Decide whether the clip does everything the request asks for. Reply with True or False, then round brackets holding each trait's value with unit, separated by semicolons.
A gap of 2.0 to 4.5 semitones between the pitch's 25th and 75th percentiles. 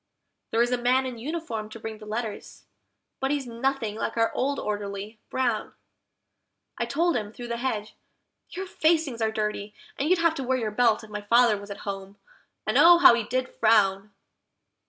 True (3.6 semitones)